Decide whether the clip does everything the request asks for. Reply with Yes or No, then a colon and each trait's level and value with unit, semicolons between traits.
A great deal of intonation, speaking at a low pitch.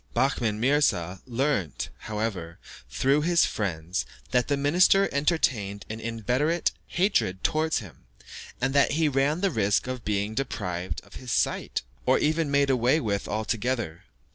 Yes: wide, 6.0 semitones; low, 125 Hz